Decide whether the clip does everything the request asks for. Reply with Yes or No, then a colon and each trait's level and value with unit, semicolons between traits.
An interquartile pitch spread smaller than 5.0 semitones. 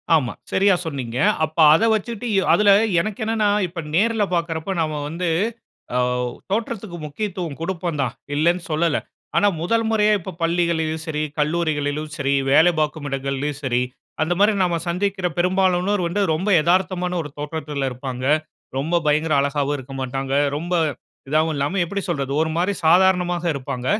Yes: average, 4.2 semitones